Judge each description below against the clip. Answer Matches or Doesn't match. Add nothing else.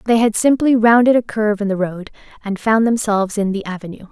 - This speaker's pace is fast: Matches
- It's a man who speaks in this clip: Doesn't match